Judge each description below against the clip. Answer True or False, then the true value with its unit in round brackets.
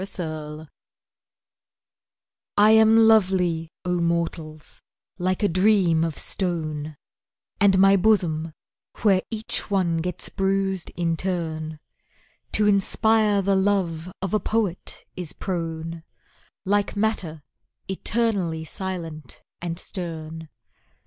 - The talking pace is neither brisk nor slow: False (105 wpm)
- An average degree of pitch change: True (3.5 semitones)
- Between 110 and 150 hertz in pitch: False (180 Hz)